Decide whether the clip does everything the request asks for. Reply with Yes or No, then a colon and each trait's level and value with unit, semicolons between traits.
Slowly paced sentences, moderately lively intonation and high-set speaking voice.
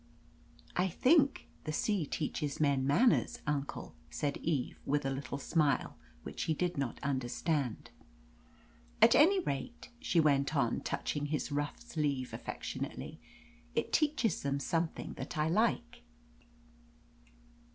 No: slow, 125 wpm; average, 3.8 semitones; medium, 150 Hz